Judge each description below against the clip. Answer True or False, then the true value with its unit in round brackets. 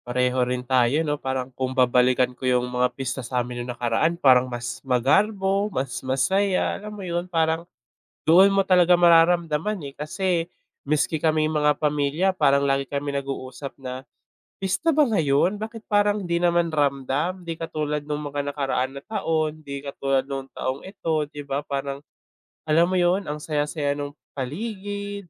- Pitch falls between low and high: True (150 Hz)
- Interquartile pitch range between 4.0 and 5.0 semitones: True (4.7 semitones)